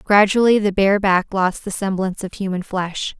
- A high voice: Yes, high, 195 Hz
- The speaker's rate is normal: Yes, average, 190 wpm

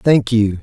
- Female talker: No, male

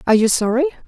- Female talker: Yes, female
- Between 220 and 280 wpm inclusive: No, fast, 205 wpm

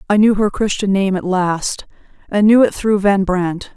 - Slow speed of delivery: No, fast, 205 wpm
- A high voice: Yes, high, 200 Hz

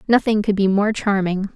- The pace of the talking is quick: No, average, 195 wpm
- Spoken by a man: No, female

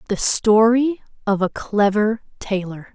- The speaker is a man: No, female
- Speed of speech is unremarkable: No, slow, 120 wpm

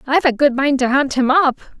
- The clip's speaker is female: Yes, female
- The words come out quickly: Yes, fast, 265 wpm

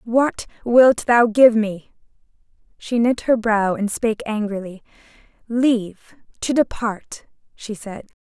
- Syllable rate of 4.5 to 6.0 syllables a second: No, 3.9 syllables/s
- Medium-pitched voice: No, high, 225 Hz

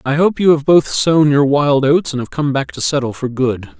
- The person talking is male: Yes, male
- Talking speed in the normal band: No, fast, 270 wpm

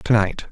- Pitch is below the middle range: Yes, low, 105 Hz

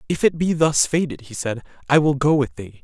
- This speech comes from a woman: No, male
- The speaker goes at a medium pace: No, fast, 255 wpm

